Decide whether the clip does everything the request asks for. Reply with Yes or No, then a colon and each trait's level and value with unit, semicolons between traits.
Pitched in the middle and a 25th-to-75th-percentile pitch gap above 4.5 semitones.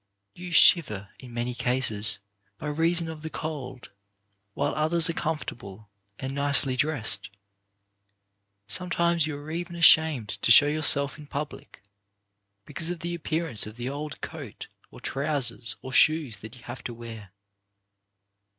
Yes: medium, 145 Hz; average, 5.0 semitones